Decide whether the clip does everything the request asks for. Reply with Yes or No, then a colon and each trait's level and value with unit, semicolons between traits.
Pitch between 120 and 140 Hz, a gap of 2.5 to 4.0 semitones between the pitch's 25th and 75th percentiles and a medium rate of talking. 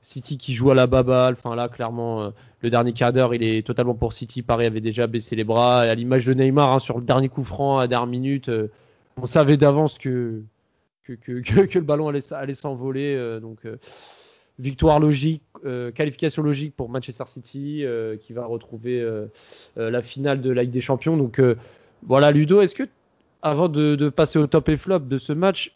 Yes: low, 130 Hz; average, 3.5 semitones; average, 190 wpm